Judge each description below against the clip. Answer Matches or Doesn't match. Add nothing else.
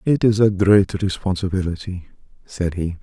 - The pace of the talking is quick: Doesn't match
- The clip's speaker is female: Doesn't match